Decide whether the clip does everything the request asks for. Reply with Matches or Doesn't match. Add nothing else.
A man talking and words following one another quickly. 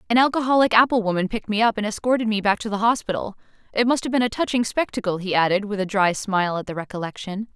Doesn't match